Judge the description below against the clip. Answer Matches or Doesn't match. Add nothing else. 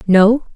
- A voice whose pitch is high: Matches